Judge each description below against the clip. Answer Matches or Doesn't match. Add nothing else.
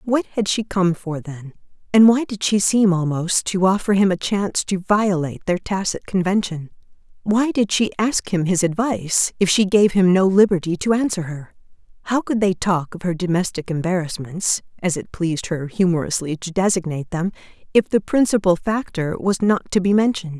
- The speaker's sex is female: Matches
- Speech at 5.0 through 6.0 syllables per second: Matches